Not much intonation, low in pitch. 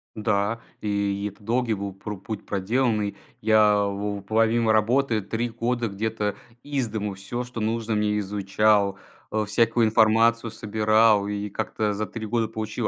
Yes: narrow, 2.0 semitones; low, 110 Hz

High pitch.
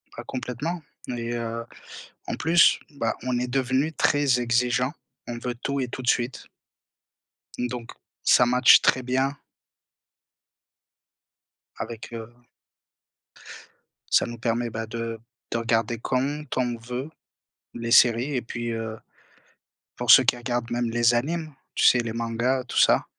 No: low, 120 Hz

